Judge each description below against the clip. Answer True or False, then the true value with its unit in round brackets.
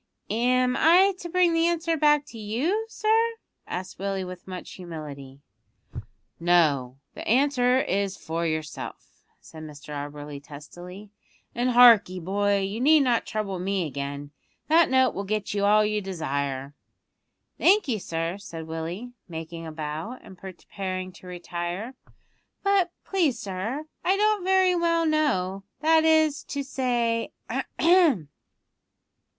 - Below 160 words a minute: True (140 wpm)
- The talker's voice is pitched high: True (205 Hz)